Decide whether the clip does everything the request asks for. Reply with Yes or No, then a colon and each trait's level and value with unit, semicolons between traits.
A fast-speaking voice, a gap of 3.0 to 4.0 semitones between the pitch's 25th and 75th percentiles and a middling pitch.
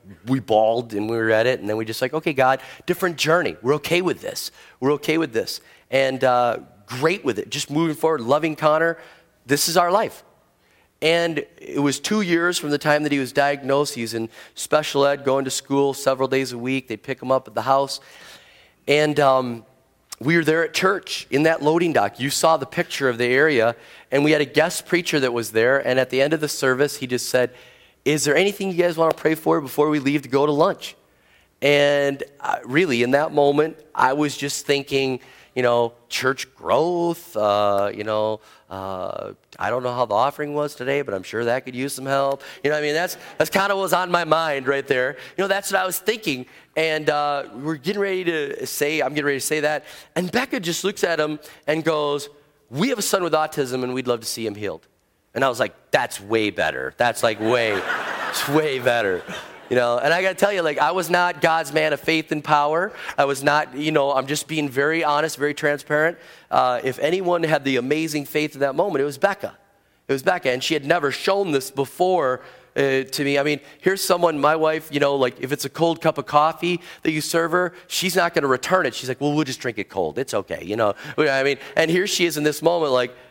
Yes: fast, 235 wpm; average, 3.6 semitones; medium, 145 Hz